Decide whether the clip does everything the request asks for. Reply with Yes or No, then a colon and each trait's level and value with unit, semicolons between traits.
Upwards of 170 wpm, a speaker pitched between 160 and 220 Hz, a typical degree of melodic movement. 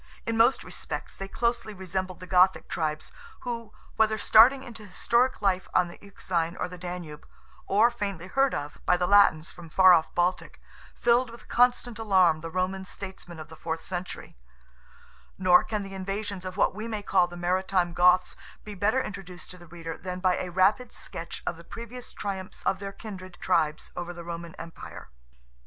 Yes: average, 185 wpm; medium, 185 Hz; average, 3.3 semitones